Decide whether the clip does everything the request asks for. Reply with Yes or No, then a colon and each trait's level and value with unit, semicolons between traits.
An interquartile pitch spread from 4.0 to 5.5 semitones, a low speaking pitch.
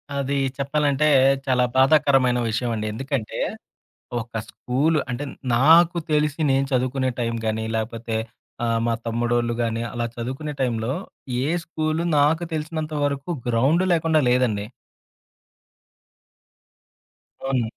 Yes: average, 4.3 semitones; low, 130 Hz